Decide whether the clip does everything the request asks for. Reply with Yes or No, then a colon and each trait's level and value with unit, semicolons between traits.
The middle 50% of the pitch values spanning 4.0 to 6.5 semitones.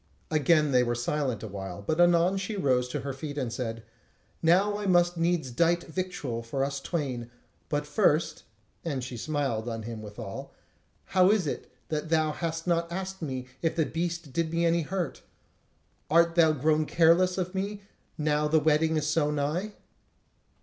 Yes: average, 4.3 semitones